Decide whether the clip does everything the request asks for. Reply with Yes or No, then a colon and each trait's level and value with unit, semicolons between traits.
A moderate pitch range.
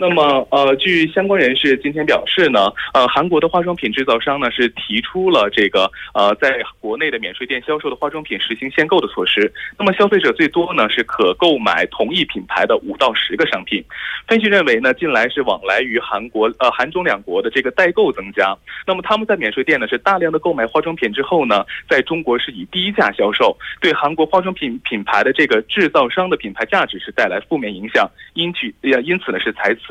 No: wide, 6.3 semitones